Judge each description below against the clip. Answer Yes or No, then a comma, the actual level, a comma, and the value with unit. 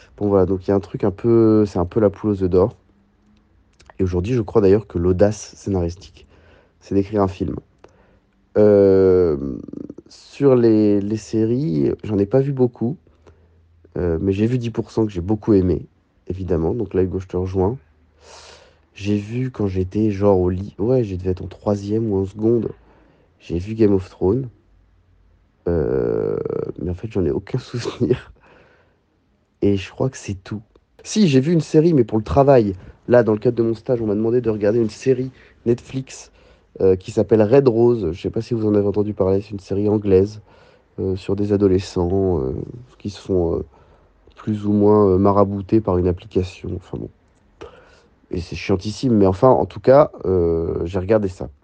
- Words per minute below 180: No, average, 190 wpm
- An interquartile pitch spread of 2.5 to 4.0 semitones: Yes, average, 3.5 semitones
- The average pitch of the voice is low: Yes, low, 100 Hz